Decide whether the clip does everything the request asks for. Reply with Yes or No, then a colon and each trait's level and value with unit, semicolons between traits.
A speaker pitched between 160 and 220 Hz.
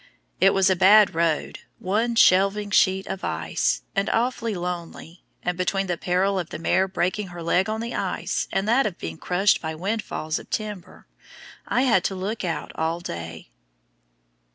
Yes: high, 190 Hz